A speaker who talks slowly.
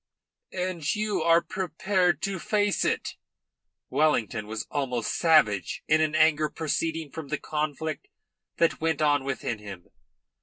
Yes: slow, 130 wpm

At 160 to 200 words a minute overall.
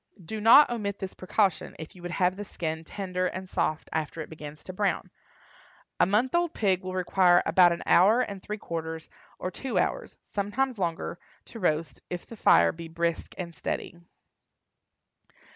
Yes: average, 165 wpm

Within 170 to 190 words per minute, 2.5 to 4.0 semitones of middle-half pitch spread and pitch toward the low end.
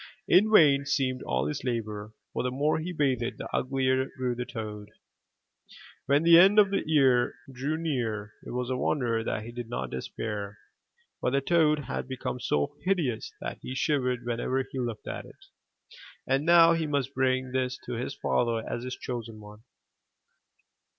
Yes: average, 175 wpm; average, 3.6 semitones; low, 130 Hz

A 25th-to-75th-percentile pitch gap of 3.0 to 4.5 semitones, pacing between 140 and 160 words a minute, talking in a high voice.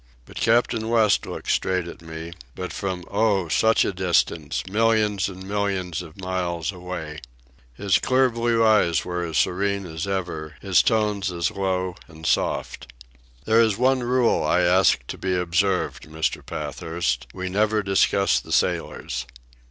No: average, 3.6 semitones; average, 150 wpm; very low, 95 Hz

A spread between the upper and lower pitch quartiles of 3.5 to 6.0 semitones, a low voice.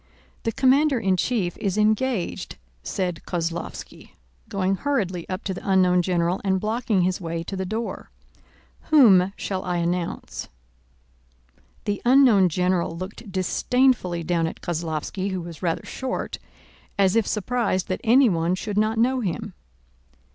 No: average, 3.9 semitones; high, 190 Hz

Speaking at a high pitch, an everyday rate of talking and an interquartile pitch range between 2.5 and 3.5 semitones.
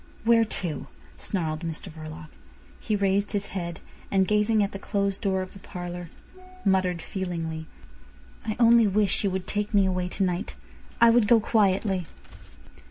Yes: high, 195 Hz; average, 160 wpm; average, 2.8 semitones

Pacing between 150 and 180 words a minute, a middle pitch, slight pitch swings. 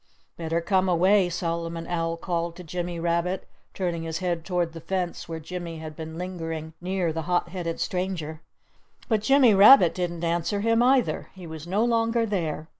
Yes: average, 175 wpm; medium, 175 Hz; narrow, 2.3 semitones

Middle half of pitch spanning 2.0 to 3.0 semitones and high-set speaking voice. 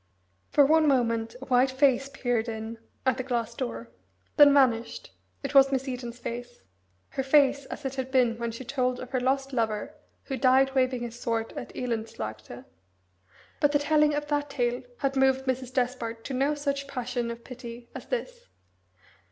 Yes: narrow, 2.6 semitones; very high, 255 Hz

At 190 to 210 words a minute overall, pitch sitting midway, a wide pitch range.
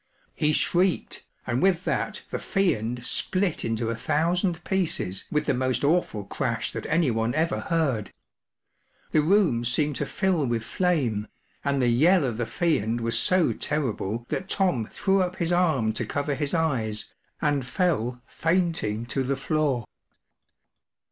No: average, 150 wpm; medium, 145 Hz; wide, 6.6 semitones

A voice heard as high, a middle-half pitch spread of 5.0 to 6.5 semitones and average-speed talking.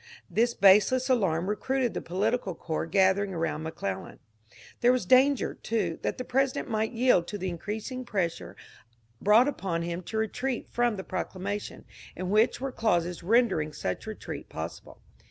Yes: high, 205 Hz; wide, 5.5 semitones; average, 160 wpm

